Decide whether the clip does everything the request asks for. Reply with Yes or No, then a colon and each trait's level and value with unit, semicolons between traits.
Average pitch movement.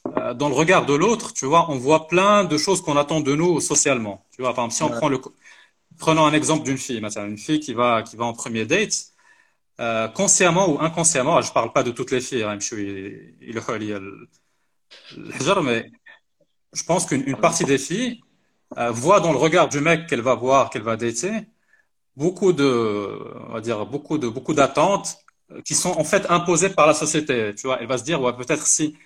No: wide, 5.8 semitones